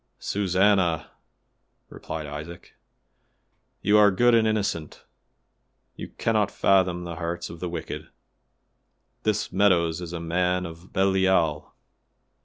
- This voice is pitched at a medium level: No, very low, 90 Hz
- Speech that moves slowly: Yes, slow, 110 wpm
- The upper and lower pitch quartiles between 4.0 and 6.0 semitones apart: No, average, 3.1 semitones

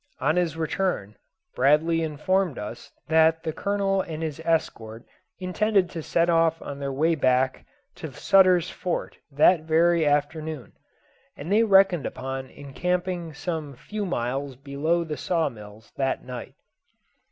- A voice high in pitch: No, medium, 160 Hz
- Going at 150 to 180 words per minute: No, average, 140 wpm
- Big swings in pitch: No, average, 4.2 semitones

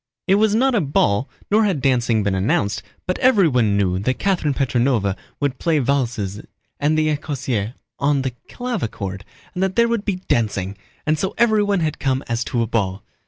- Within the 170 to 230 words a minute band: Yes, average, 180 wpm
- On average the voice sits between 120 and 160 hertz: Yes, medium, 140 Hz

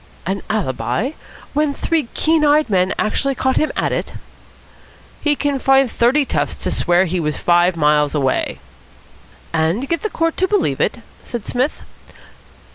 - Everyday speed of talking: Yes, average, 155 wpm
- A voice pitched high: Yes, high, 245 Hz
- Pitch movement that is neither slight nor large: No, wide, 9.0 semitones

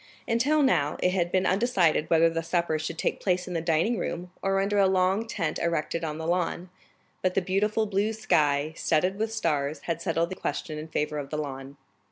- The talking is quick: Yes, fast, 210 wpm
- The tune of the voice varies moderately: Yes, average, 3.6 semitones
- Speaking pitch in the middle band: Yes, medium, 175 Hz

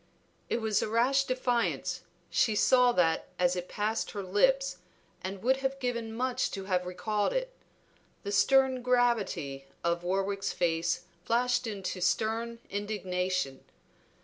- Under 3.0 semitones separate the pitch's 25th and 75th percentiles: No, average, 5.2 semitones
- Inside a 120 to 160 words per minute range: Yes, average, 140 wpm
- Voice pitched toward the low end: No, high, 215 Hz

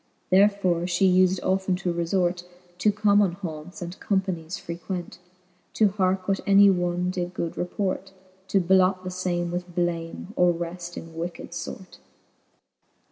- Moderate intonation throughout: No, narrow, 1.6 semitones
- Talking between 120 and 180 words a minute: Yes, average, 140 wpm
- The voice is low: No, medium, 180 Hz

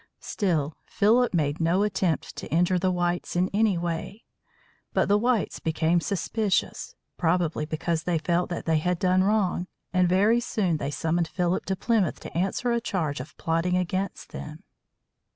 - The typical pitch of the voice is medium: Yes, medium, 180 Hz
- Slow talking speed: No, average, 165 wpm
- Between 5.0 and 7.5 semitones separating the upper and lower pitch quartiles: No, average, 3.0 semitones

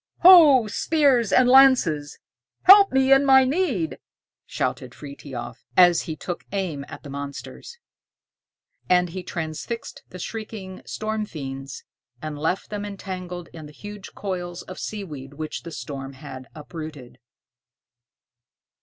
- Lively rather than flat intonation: Yes, wide, 7.0 semitones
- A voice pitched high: No, medium, 180 Hz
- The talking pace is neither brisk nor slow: No, slow, 130 wpm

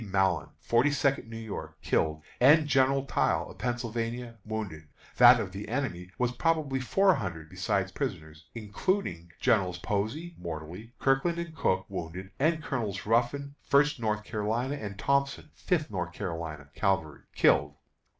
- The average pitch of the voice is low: Yes, low, 110 Hz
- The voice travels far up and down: Yes, wide, 6.8 semitones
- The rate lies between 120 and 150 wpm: Yes, average, 140 wpm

